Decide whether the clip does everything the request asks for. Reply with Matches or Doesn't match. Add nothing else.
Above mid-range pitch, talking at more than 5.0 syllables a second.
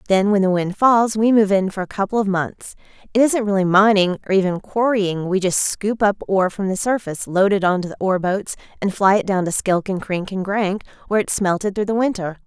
Matches